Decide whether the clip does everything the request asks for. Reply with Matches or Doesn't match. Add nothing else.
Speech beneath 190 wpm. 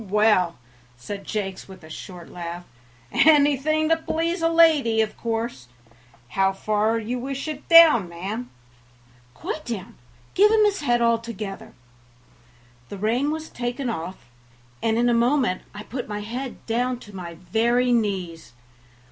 Matches